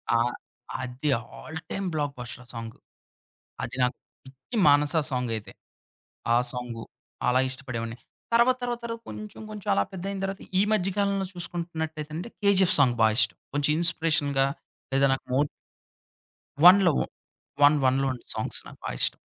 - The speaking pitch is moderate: Yes, medium, 145 Hz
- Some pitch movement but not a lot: No, wide, 7.0 semitones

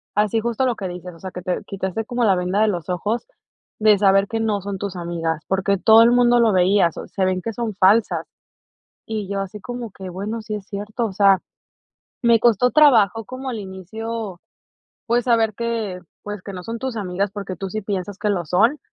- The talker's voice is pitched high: Yes, high, 205 Hz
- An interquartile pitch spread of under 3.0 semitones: No, average, 3.3 semitones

